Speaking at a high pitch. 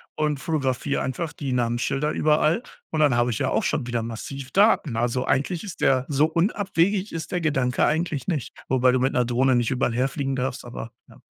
No: low, 135 Hz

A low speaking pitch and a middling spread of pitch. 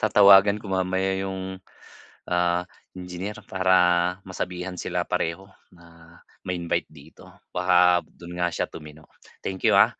No: very low, 90 Hz; narrow, 1.5 semitones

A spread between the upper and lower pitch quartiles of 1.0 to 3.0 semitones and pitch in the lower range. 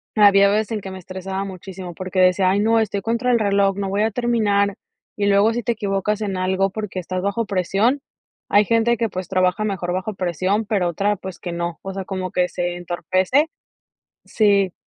No: narrow, 2.4 semitones; high, 195 Hz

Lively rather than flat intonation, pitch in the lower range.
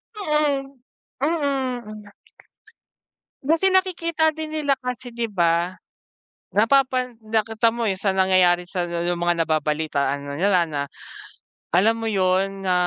No: wide, 7.4 semitones; high, 215 Hz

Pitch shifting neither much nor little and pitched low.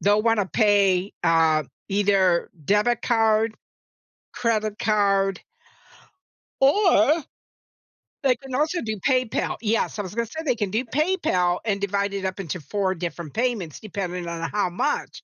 No: average, 3.7 semitones; high, 205 Hz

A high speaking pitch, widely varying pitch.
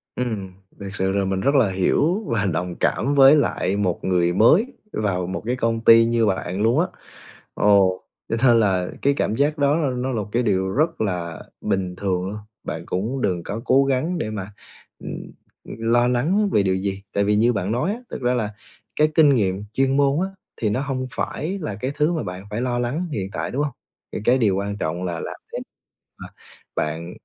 No: low, 110 Hz; wide, 5.8 semitones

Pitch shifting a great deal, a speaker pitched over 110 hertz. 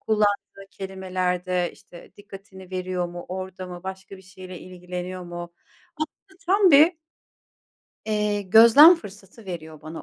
No: narrow, 2.4 semitones; high, 190 Hz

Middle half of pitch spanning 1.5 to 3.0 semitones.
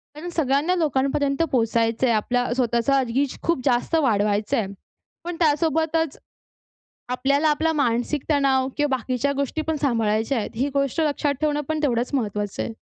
No: average, 4.0 semitones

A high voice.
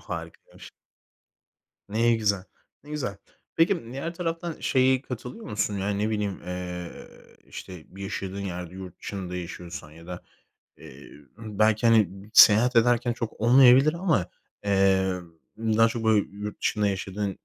No: low, 105 Hz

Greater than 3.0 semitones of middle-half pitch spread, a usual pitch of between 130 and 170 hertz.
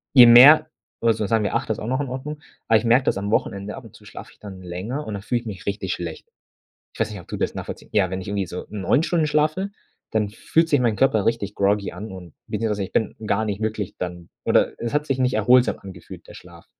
No: average, 4.2 semitones; low, 110 Hz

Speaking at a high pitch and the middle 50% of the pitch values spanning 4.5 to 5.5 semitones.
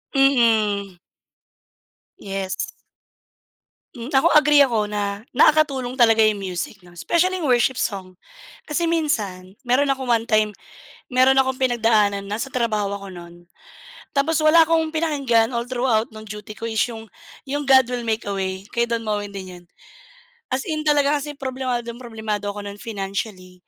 Yes: high, 230 Hz; average, 4.8 semitones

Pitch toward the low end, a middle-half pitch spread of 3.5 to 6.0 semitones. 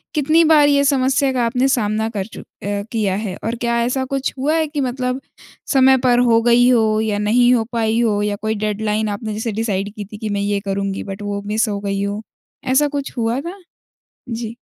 No: high, 225 Hz; average, 3.8 semitones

